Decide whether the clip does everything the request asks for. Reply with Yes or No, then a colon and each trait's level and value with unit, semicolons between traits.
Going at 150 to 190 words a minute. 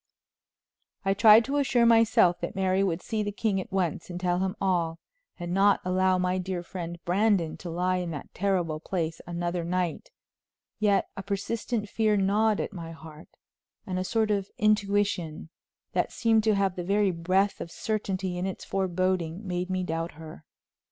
Yes: average, 175 wpm